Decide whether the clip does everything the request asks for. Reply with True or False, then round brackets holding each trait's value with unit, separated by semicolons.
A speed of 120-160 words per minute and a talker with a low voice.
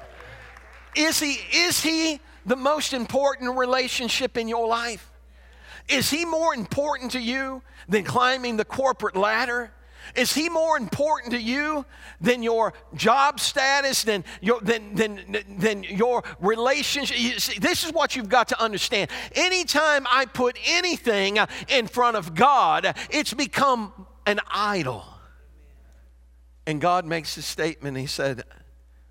False (140 wpm; 240 Hz)